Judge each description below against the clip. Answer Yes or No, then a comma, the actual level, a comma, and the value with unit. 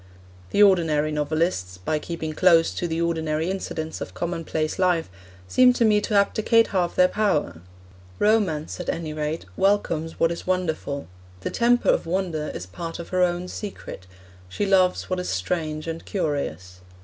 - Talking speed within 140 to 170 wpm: Yes, average, 160 wpm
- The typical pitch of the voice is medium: Yes, medium, 170 Hz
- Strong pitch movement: No, average, 3.3 semitones